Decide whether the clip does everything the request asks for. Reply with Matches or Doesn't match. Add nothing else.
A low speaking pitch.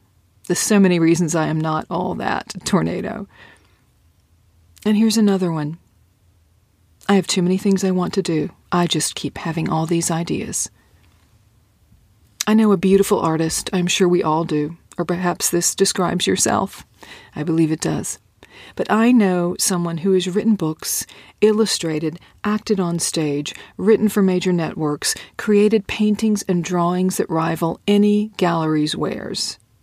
Doesn't match